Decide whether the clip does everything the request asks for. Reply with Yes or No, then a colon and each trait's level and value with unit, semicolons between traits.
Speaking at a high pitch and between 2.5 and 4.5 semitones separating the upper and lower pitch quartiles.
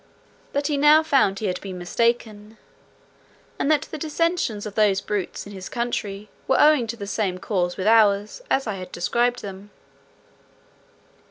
No: high, 215 Hz; average, 5.0 semitones